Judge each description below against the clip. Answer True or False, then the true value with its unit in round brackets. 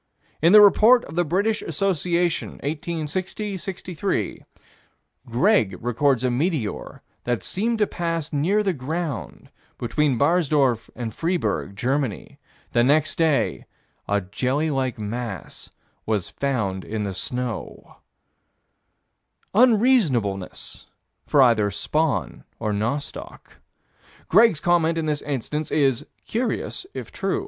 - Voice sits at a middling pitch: True (150 Hz)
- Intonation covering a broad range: True (6.6 semitones)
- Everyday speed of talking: False (115 wpm)